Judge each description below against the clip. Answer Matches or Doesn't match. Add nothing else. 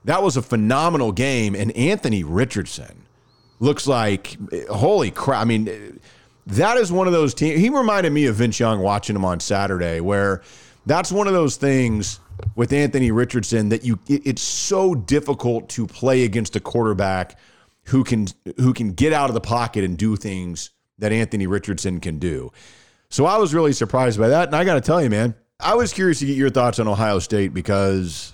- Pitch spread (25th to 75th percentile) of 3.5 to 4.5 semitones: Doesn't match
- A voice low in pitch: Matches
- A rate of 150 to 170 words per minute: Doesn't match